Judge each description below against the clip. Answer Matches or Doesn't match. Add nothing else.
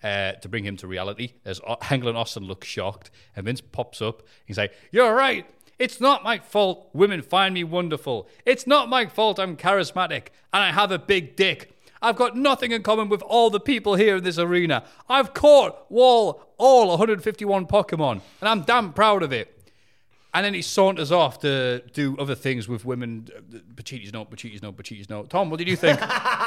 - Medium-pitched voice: Matches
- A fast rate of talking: Doesn't match